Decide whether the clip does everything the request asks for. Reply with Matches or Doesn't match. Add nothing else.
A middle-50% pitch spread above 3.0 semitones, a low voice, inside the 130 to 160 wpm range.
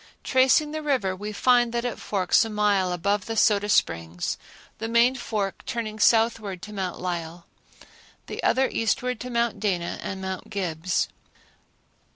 Doesn't match